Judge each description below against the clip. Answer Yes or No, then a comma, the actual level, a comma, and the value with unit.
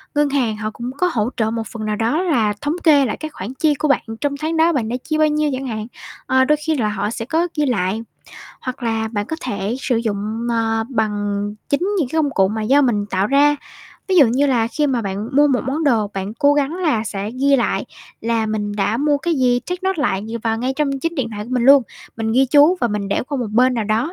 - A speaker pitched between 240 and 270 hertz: Yes, high, 245 Hz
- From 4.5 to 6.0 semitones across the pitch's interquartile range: Yes, average, 4.9 semitones